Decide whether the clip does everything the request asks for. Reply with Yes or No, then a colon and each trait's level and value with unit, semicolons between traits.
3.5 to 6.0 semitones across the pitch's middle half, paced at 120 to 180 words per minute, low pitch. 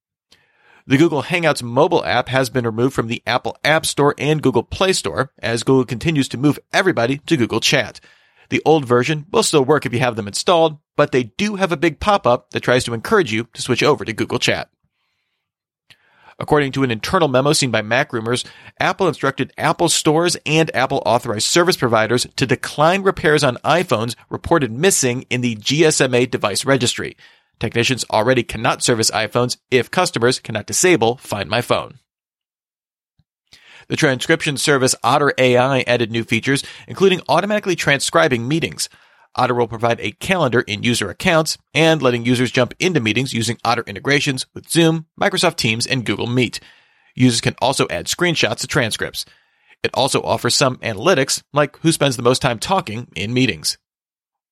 Yes: average, 4.5 semitones; average, 170 wpm; low, 130 Hz